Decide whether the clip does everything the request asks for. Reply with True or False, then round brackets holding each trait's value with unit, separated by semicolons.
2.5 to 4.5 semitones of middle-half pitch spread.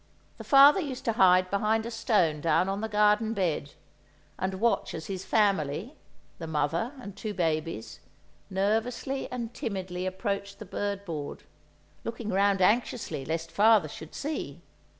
False (4.9 semitones)